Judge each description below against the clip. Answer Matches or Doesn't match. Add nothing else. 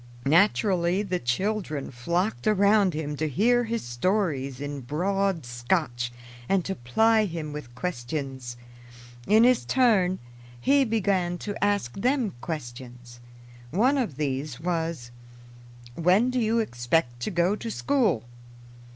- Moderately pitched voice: Matches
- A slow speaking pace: Matches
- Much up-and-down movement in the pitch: Matches